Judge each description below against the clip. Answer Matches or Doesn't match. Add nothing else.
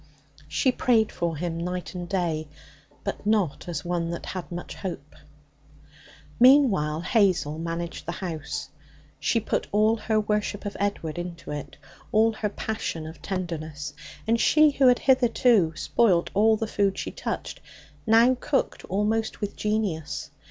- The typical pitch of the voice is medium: Doesn't match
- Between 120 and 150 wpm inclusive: Matches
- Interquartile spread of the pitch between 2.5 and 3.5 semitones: Doesn't match